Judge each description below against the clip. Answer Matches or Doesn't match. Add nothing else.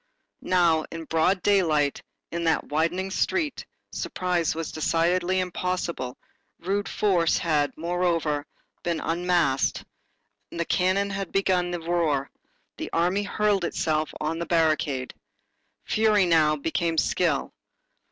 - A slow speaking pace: Matches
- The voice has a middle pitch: Matches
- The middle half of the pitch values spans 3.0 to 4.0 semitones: Doesn't match